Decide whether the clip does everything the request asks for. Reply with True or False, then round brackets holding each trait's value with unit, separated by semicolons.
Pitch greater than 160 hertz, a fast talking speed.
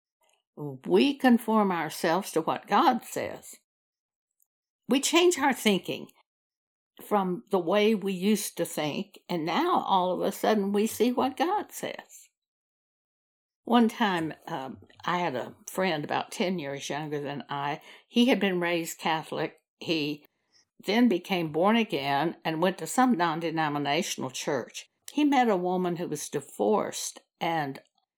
False (185 Hz; 145 wpm)